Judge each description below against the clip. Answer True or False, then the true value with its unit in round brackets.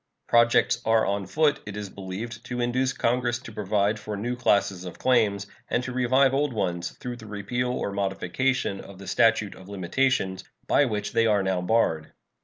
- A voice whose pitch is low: True (110 Hz)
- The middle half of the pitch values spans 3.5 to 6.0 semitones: True (3.9 semitones)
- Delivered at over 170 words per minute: True (185 wpm)